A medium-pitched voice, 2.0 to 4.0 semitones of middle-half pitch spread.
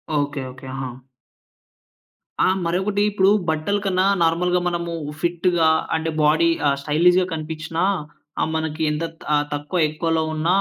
Yes: medium, 165 Hz; narrow, 2.4 semitones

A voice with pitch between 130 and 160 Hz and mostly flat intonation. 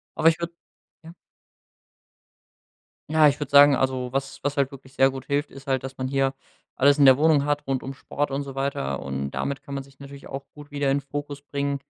Yes: medium, 140 Hz; narrow, 1.3 semitones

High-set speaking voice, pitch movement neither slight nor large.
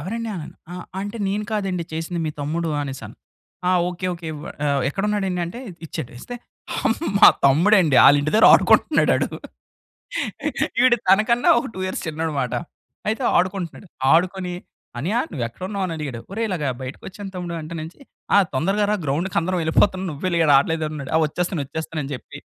No: medium, 175 Hz; average, 4.1 semitones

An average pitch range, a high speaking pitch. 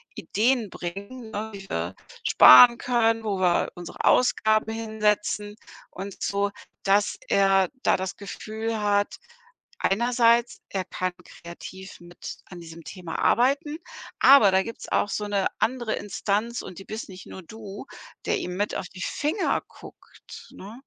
Yes: average, 3.1 semitones; high, 205 Hz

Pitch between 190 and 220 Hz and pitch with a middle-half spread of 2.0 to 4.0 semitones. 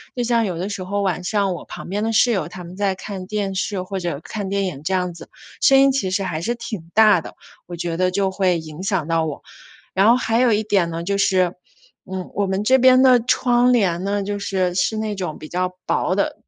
Yes: high, 195 Hz; average, 3.1 semitones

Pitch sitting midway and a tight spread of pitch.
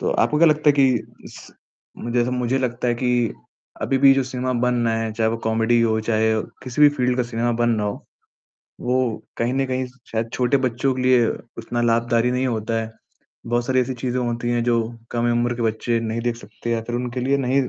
No: low, 120 Hz; narrow, 1.6 semitones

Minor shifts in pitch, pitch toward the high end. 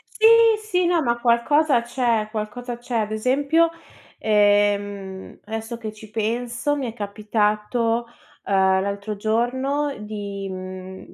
No: average, 3.1 semitones; high, 220 Hz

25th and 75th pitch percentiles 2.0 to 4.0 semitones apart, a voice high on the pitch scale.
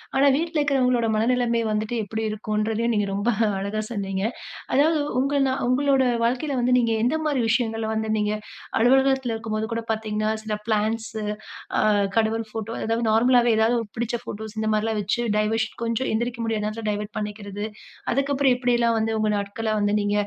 Yes: narrow, 2.4 semitones; high, 225 Hz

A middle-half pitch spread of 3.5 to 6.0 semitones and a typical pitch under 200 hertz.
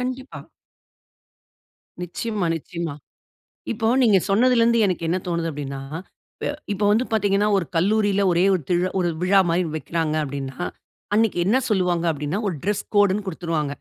Yes: average, 4.0 semitones; medium, 185 Hz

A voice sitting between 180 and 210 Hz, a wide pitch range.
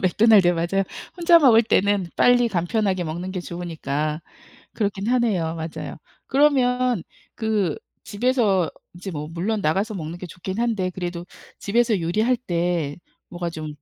No: high, 190 Hz; average, 4.8 semitones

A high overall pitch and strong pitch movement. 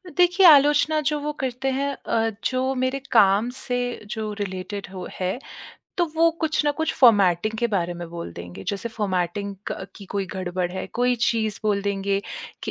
Yes: high, 220 Hz; wide, 5.8 semitones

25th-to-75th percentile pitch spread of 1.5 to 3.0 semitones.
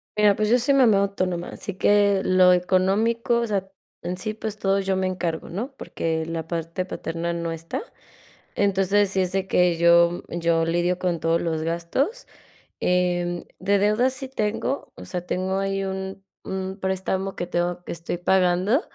Yes: narrow, 2.6 semitones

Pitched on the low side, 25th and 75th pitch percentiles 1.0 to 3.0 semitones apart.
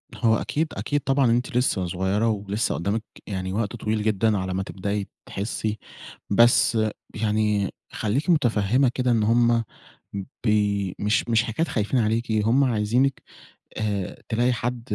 Yes: low, 110 Hz; average, 2.7 semitones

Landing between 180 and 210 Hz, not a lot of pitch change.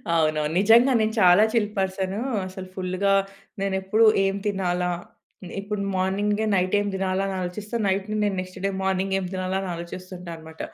Yes: high, 190 Hz; narrow, 1.6 semitones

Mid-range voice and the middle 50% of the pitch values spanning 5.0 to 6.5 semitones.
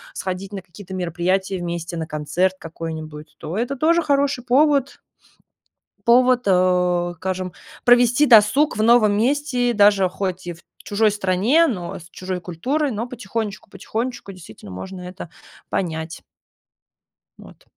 No: high, 195 Hz; wide, 5.5 semitones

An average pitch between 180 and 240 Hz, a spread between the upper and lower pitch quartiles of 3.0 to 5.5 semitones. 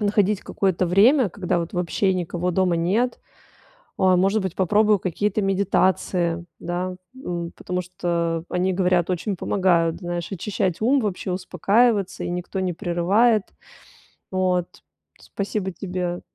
No: medium, 185 Hz; narrow, 2.4 semitones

